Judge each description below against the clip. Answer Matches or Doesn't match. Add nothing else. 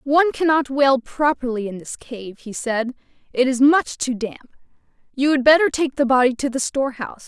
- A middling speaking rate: Matches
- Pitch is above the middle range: Matches